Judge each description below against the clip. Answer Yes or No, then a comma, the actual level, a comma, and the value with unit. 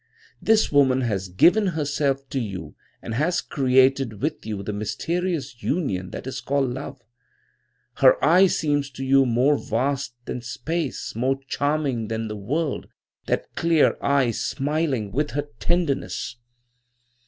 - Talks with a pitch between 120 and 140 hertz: Yes, low, 135 Hz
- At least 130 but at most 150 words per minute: Yes, average, 140 wpm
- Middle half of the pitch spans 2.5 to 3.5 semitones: No, average, 4.1 semitones